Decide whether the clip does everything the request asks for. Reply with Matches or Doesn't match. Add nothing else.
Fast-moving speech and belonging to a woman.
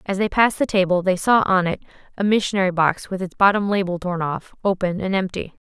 Matches